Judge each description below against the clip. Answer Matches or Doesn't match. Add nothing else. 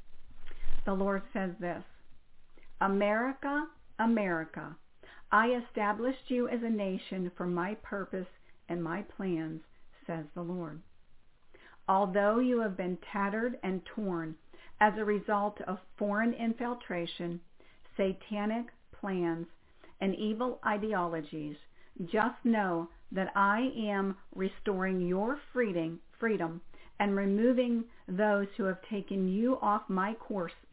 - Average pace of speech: Doesn't match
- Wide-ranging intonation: Doesn't match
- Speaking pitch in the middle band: Doesn't match